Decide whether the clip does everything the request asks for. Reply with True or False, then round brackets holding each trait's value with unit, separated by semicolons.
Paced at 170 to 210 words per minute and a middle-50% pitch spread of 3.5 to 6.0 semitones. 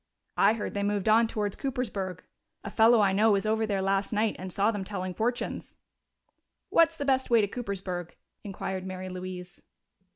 False (175 wpm; 2.9 semitones)